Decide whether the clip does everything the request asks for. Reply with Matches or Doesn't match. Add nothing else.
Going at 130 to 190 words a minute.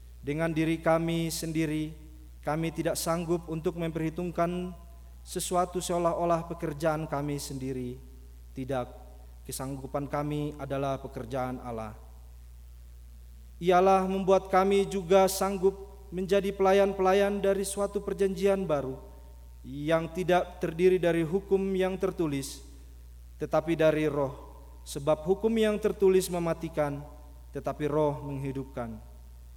Doesn't match